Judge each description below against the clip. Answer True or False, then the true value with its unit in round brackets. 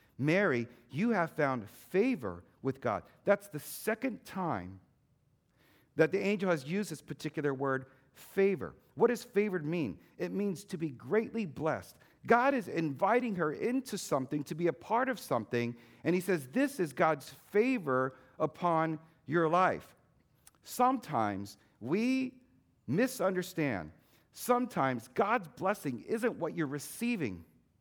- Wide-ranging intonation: True (7.3 semitones)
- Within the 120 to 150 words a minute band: True (135 wpm)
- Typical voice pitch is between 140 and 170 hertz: True (160 Hz)